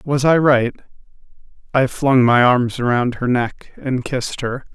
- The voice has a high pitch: No, low, 125 Hz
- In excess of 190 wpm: No, average, 165 wpm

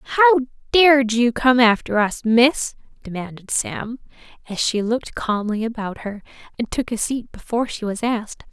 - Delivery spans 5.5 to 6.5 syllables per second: Yes, 5.7 syllables/s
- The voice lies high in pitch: Yes, high, 235 Hz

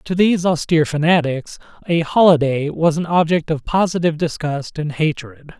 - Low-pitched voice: No, medium, 160 Hz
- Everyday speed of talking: Yes, average, 150 wpm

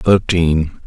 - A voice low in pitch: Yes, very low, 85 Hz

